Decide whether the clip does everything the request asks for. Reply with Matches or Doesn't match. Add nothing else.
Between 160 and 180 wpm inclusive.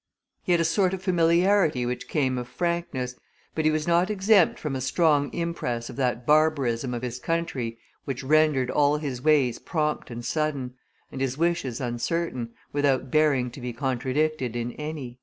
Matches